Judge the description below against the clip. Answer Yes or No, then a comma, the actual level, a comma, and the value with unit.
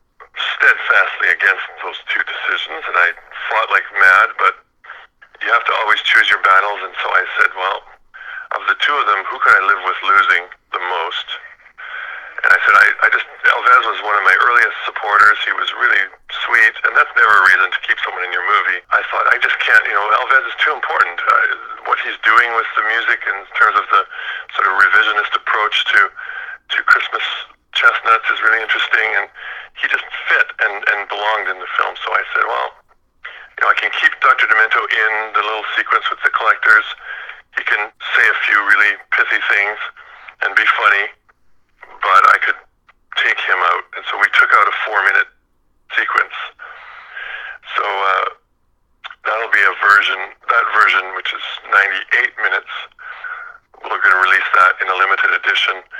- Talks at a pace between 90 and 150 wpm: No, average, 185 wpm